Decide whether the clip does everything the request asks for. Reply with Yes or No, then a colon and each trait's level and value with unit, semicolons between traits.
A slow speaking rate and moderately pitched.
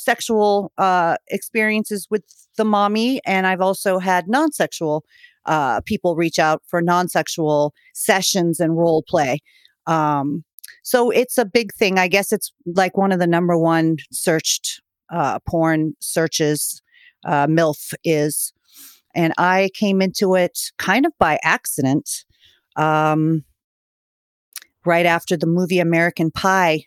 Yes: slow, 130 wpm; medium, 180 Hz